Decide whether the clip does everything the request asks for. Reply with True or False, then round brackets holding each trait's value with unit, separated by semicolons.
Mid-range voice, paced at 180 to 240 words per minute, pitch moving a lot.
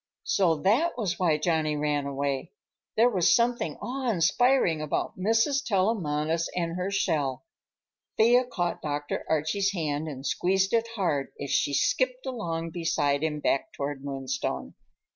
False (165 Hz; 145 wpm; 6.8 semitones)